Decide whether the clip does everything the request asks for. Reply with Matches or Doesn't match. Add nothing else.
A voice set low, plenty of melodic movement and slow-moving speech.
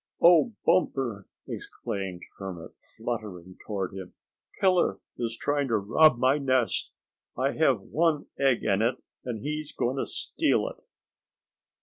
Matches